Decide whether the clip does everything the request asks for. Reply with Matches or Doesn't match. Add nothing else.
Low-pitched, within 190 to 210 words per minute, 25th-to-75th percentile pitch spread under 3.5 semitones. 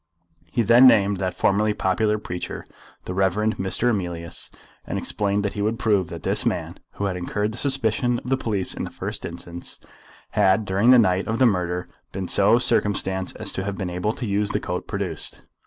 Matches